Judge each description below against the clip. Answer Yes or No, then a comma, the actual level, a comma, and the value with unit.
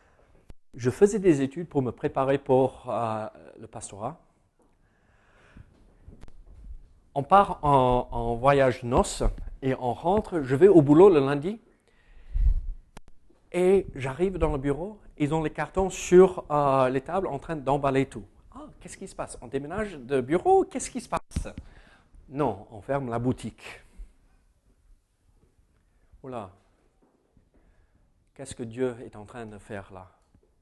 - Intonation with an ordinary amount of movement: No, wide, 7.1 semitones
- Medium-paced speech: No, slow, 140 wpm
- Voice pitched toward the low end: Yes, low, 130 Hz